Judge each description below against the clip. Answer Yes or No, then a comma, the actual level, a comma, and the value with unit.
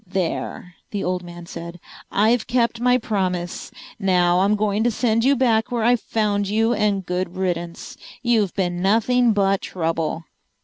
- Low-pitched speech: No, high, 200 Hz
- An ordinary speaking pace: Yes, average, 160 wpm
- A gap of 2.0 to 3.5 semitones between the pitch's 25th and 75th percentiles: No, average, 4.1 semitones